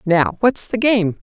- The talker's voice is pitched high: Yes, high, 210 Hz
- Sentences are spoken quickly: No, average, 190 wpm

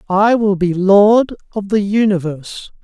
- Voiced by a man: Yes, male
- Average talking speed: Yes, average, 150 wpm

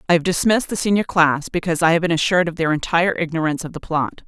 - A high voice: No, medium, 170 Hz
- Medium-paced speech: No, fast, 255 wpm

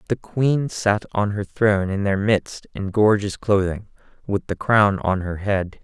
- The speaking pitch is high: No, low, 100 Hz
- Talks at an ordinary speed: Yes, average, 185 wpm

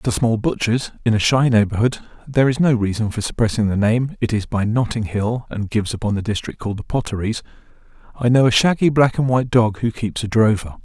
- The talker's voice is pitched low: Yes, low, 115 Hz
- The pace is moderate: No, fast, 225 wpm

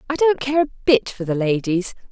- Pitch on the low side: No, high, 235 Hz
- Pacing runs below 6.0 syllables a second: Yes, 5.6 syllables/s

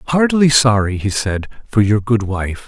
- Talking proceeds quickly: No, average, 180 wpm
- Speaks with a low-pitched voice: Yes, low, 115 Hz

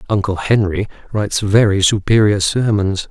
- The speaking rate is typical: No, slow, 115 wpm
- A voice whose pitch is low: Yes, low, 100 Hz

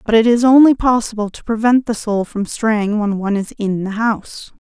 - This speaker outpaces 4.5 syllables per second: Yes, 5.2 syllables/s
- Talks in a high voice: Yes, high, 220 Hz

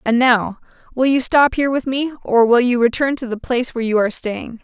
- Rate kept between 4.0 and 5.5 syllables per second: No, 5.9 syllables/s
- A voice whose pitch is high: Yes, high, 245 Hz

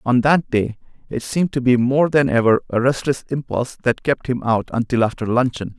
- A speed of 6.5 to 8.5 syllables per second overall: No, 5.6 syllables/s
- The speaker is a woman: No, male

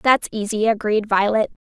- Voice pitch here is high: Yes, high, 215 Hz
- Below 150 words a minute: Yes, average, 140 wpm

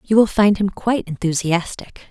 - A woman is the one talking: Yes, female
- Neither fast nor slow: Yes, average, 170 wpm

